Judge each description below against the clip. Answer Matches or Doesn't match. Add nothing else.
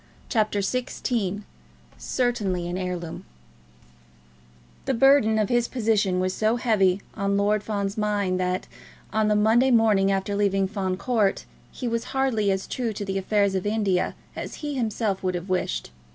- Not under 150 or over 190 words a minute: Matches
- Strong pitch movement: Doesn't match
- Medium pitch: Doesn't match